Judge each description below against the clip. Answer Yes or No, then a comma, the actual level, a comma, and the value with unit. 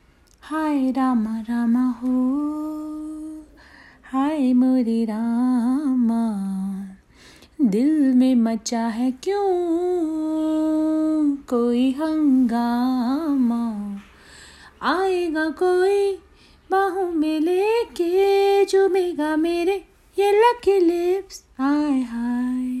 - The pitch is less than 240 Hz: No, very high, 295 Hz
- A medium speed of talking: No, slow, 70 wpm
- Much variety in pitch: Yes, wide, 5.9 semitones